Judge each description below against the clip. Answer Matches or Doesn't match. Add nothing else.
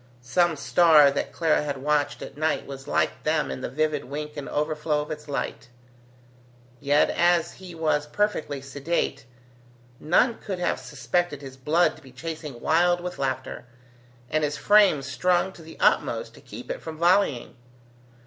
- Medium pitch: Matches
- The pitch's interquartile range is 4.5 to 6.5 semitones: Doesn't match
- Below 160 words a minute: Doesn't match